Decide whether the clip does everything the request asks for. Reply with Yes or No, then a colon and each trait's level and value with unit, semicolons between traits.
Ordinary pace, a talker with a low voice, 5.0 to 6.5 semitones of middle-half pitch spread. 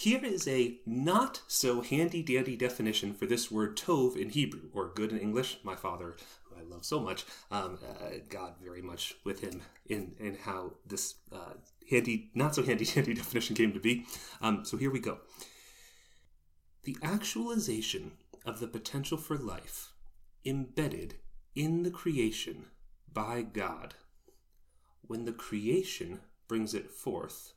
Yes: average, 150 wpm; low, 115 Hz; average, 5.3 semitones